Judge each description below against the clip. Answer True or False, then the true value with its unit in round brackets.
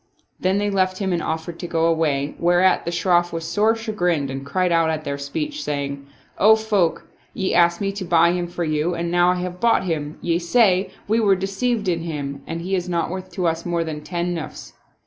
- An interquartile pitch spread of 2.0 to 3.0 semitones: True (2.5 semitones)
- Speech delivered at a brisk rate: True (225 wpm)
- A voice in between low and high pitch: True (175 Hz)